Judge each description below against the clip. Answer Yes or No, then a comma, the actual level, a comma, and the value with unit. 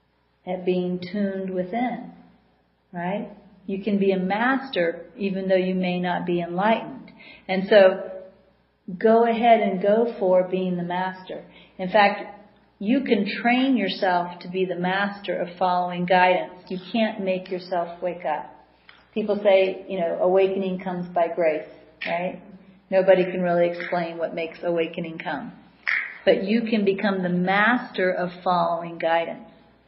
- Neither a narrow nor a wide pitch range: No, narrow, 2.3 semitones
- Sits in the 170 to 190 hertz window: Yes, medium, 185 Hz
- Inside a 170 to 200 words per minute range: No, average, 145 wpm